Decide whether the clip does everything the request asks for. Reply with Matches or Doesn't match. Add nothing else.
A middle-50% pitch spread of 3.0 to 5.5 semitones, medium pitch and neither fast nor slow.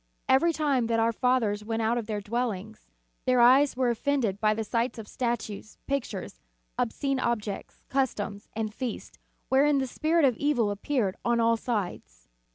Doesn't match